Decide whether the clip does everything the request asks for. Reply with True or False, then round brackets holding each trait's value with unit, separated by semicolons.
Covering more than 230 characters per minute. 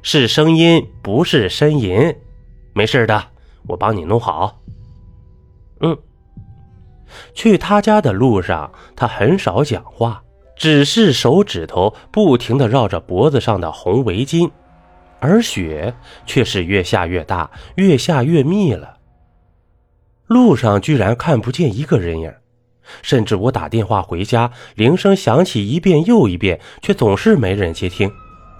False (195 characters per minute)